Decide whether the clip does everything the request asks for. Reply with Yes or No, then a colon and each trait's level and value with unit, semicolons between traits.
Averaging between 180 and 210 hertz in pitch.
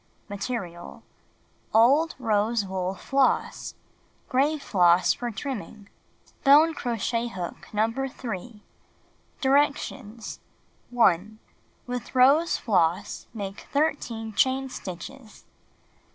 No: high, 230 Hz